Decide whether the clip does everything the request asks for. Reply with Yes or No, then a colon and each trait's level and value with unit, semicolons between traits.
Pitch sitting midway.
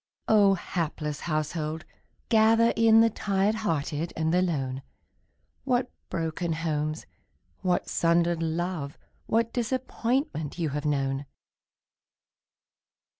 Yes: medium, 170 Hz